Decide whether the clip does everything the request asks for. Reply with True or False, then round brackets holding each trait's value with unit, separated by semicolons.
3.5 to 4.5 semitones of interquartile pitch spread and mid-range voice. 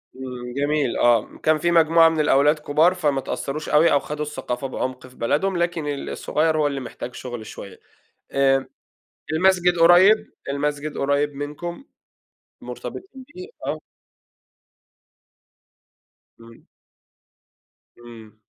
True (4.0 semitones; 145 Hz)